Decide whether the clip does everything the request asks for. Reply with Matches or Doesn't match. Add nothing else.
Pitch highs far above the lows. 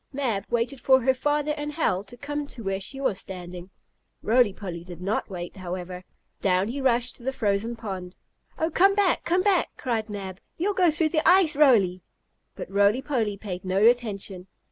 Matches